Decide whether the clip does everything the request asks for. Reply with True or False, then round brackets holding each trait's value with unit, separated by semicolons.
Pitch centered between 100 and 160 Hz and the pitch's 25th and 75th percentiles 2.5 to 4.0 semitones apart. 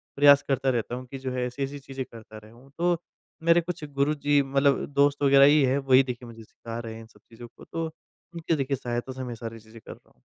True (135 Hz; 2.9 semitones)